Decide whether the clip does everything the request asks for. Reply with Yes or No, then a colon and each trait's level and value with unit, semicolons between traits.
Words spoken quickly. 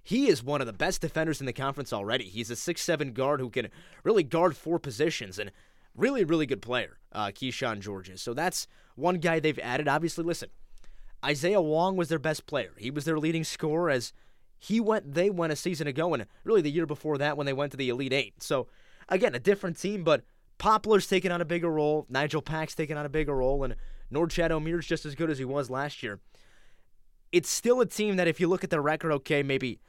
Yes: fast, 225 wpm